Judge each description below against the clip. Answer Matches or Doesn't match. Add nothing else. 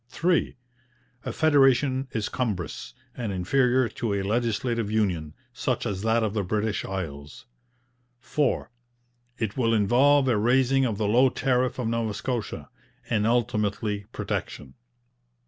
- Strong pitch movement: Doesn't match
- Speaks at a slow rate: Matches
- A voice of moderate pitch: Doesn't match